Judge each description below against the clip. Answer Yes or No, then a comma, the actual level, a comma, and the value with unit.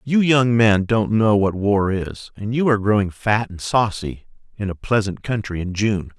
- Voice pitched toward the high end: No, low, 105 Hz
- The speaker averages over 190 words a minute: Yes, fast, 205 wpm